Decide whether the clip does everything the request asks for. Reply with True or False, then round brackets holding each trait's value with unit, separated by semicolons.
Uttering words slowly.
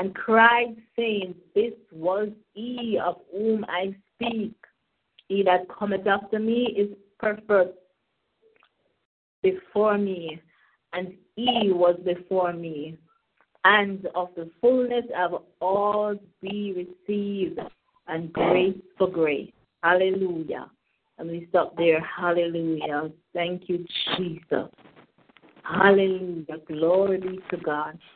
True (105 wpm)